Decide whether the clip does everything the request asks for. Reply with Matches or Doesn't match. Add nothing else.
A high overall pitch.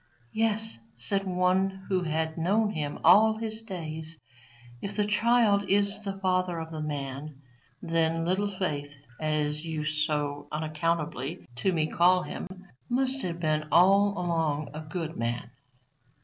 Doesn't match